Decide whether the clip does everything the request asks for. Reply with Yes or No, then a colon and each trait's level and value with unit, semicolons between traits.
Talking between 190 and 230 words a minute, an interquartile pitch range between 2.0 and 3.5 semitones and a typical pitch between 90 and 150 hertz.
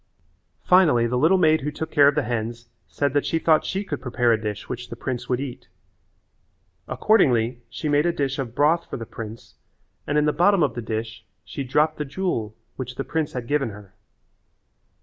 No: fast, 205 wpm; average, 4.6 semitones; low, 135 Hz